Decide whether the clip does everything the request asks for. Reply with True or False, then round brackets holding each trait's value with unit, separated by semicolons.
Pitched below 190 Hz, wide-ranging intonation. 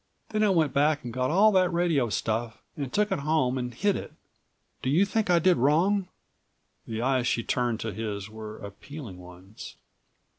True (135 Hz; 7.6 semitones)